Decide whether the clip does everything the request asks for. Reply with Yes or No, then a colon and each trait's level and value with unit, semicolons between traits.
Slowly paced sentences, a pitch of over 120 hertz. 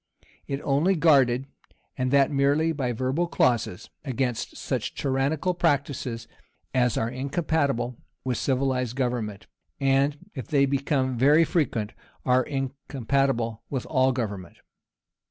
Yes: slow, 120 wpm; low, 135 Hz